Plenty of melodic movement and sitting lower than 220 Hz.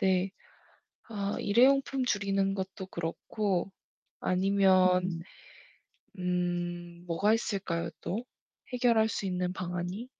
No: narrow, 2.6 semitones; high, 190 Hz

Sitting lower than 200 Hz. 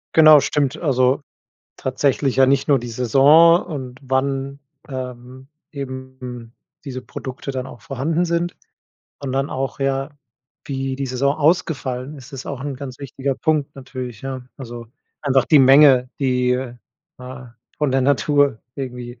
Yes: low, 135 Hz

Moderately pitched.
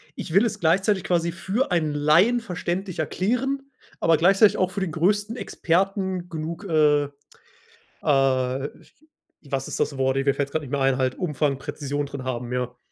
Yes: medium, 160 Hz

